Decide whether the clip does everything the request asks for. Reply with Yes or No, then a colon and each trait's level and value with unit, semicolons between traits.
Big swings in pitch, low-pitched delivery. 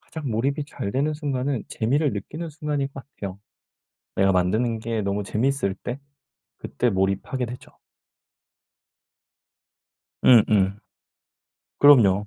Yes: wide, 5.8 semitones; low, 120 Hz